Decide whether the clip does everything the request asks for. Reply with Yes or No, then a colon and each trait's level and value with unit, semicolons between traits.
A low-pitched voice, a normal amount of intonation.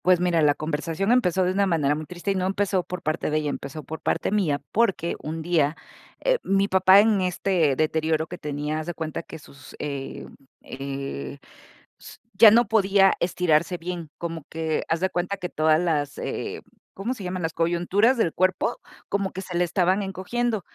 No: medium, 175 Hz; average, 3.6 semitones